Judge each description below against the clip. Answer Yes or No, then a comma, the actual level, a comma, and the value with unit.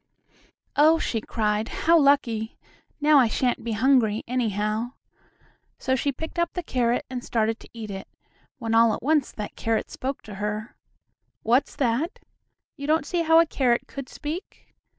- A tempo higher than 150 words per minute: Yes, average, 165 wpm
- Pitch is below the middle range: No, high, 245 Hz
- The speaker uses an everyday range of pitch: Yes, average, 4.7 semitones